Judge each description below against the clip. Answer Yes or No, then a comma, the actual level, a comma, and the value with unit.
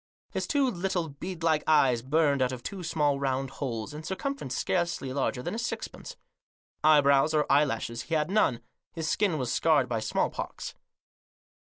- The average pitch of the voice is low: No, medium, 150 Hz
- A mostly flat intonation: No, average, 4.3 semitones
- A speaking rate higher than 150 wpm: Yes, average, 165 wpm